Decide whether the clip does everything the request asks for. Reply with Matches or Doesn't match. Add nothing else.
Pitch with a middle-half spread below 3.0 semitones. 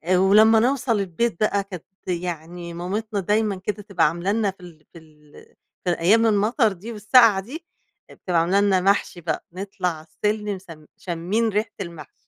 Doesn't match